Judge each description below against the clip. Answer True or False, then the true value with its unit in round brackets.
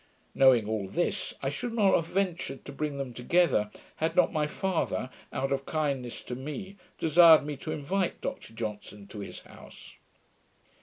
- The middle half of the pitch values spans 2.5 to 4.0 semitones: False (5.5 semitones)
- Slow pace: False (160 wpm)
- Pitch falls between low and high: True (145 Hz)